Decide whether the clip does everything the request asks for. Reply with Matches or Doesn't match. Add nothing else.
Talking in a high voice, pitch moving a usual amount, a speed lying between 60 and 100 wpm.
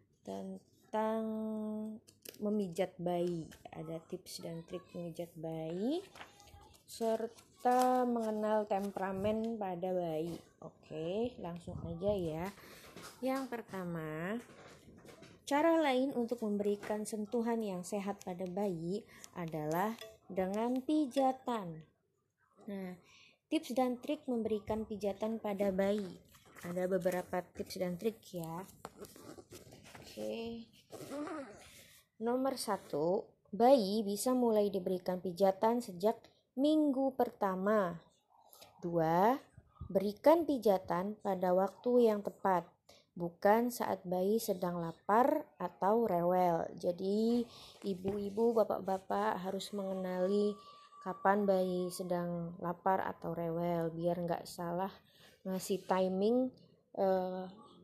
Matches